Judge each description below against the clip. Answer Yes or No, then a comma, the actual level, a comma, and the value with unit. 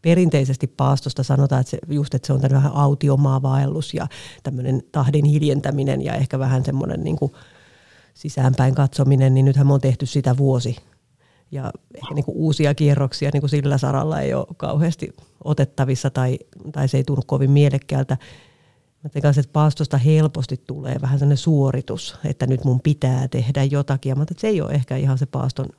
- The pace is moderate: No, fast, 175 wpm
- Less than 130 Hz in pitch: No, medium, 140 Hz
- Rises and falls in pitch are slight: Yes, narrow, 1.6 semitones